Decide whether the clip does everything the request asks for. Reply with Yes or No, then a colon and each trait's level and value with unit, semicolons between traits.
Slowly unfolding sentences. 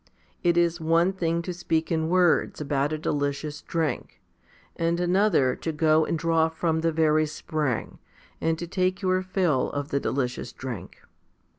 No: average, 160 wpm